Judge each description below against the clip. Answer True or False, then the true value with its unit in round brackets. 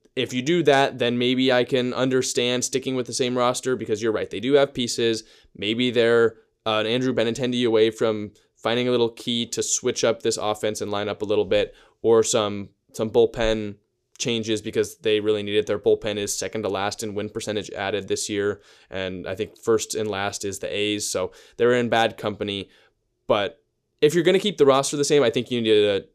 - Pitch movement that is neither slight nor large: True (3.3 semitones)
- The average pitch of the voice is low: True (115 Hz)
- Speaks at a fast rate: True (220 wpm)